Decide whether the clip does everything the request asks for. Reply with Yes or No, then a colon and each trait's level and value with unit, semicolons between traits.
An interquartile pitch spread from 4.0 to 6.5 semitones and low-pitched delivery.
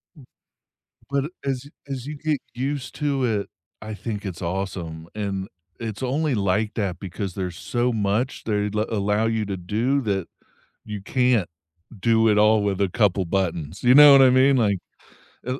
Yes: average, 4.6 semitones; low, 110 Hz